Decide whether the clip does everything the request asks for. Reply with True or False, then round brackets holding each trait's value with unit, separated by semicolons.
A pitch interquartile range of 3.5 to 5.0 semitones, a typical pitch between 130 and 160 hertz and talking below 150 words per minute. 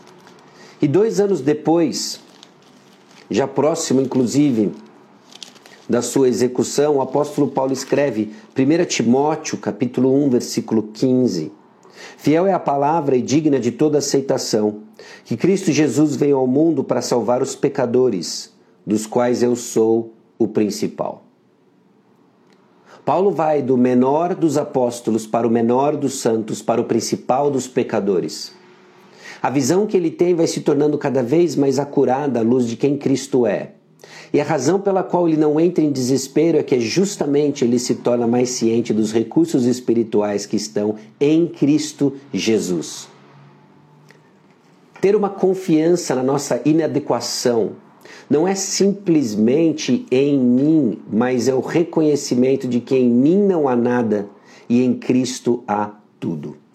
True (4.4 semitones; 135 Hz; 140 wpm)